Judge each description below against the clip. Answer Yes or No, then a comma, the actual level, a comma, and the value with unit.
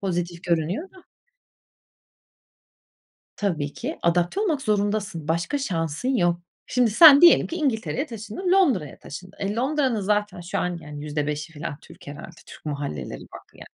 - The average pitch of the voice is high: Yes, high, 200 Hz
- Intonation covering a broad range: Yes, wide, 8.0 semitones